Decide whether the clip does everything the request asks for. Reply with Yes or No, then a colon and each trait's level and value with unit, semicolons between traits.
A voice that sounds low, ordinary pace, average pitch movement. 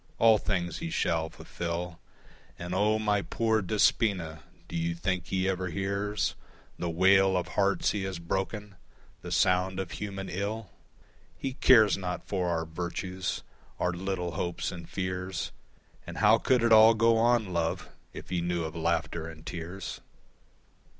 Yes: very low, 95 Hz; average, 155 wpm; average, 3.1 semitones